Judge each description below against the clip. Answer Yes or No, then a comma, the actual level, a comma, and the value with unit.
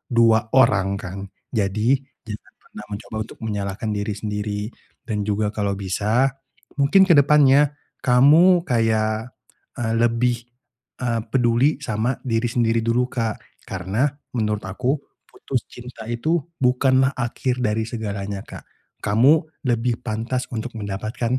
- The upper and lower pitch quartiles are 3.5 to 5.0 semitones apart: No, average, 2.9 semitones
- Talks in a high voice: No, low, 115 Hz